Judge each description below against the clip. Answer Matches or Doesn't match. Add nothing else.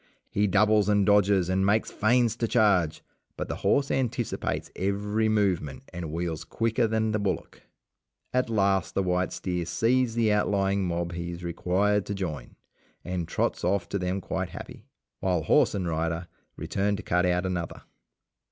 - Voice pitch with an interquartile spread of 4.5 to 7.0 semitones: Doesn't match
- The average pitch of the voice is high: Doesn't match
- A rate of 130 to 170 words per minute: Matches